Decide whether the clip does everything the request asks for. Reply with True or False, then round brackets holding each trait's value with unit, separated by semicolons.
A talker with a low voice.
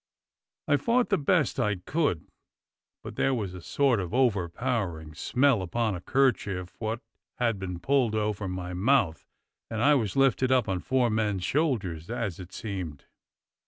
True (110 Hz)